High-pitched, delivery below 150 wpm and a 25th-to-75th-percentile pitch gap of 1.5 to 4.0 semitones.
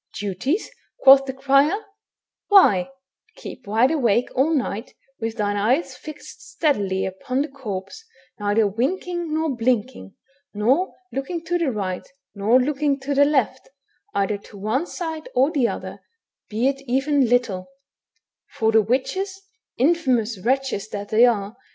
No: very high, 255 Hz; average, 140 wpm; wide, 5.6 semitones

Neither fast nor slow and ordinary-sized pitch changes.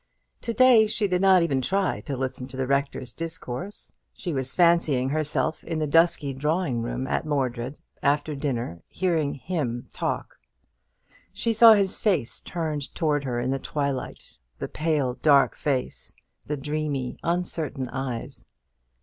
Yes: average, 150 wpm; average, 4.3 semitones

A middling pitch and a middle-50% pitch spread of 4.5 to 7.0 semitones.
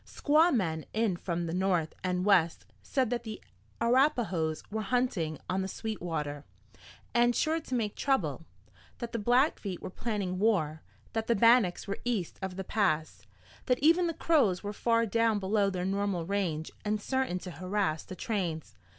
No: high, 200 Hz; average, 4.8 semitones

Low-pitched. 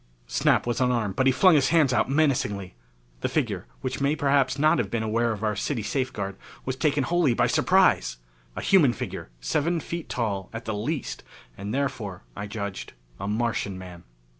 Yes: low, 120 Hz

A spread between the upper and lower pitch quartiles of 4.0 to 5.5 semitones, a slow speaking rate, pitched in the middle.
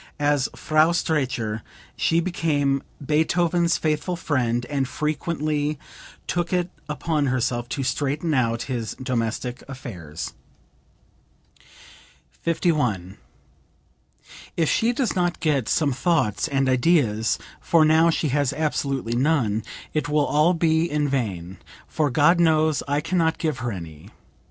Yes: average, 4.6 semitones; slow, 125 wpm; medium, 145 Hz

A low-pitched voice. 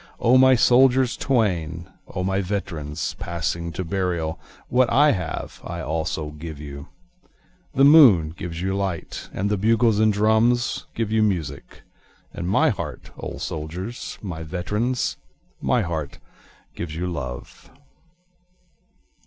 Yes: very low, 95 Hz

